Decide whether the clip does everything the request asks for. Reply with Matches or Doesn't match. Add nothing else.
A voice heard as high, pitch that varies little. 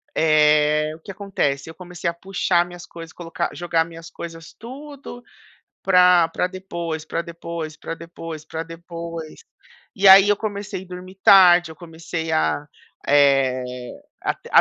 Doesn't match